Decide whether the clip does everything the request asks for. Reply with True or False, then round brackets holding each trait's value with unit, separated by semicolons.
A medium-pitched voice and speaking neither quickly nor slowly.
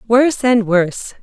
False (225 Hz; 145 wpm)